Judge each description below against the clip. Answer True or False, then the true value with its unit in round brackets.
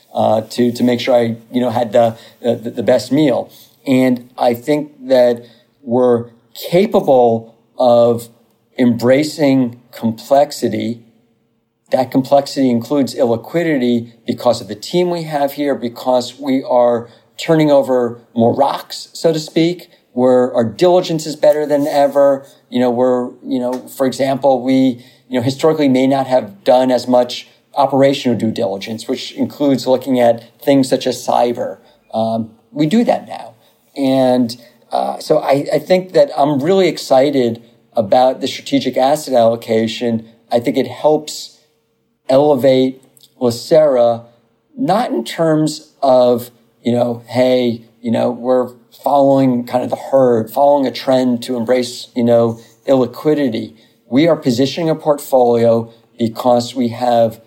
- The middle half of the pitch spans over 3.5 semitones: False (2.8 semitones)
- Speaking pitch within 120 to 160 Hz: True (125 Hz)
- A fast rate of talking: False (140 wpm)